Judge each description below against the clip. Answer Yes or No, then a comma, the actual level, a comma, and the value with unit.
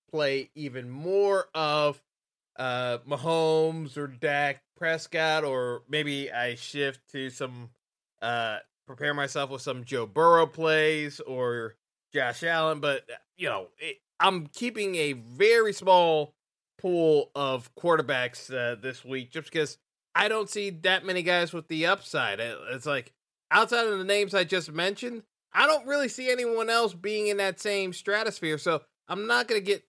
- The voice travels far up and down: Yes, wide, 6.1 semitones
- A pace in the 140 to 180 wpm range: Yes, average, 155 wpm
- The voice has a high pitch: No, medium, 160 Hz